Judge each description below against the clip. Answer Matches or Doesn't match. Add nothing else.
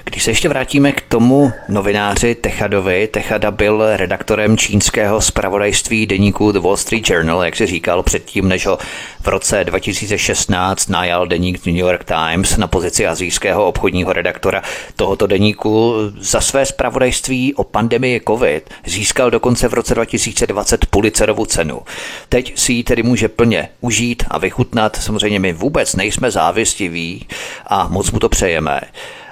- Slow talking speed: Doesn't match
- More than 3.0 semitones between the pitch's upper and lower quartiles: Matches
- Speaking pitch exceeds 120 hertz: Doesn't match